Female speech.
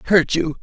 No: male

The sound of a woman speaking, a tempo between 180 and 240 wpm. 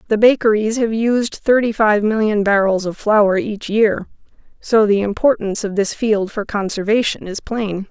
No: female; average, 165 wpm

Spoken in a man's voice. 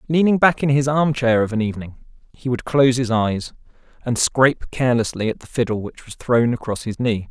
Yes: male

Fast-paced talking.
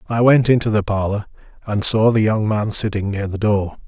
Yes: fast, 215 wpm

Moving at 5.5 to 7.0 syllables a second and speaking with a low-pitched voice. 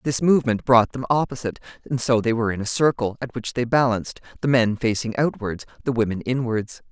Yes: 6.0 syllables/s; low, 120 Hz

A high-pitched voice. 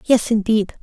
Yes: high, 220 Hz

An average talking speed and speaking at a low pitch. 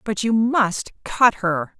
No: average, 165 wpm; high, 210 Hz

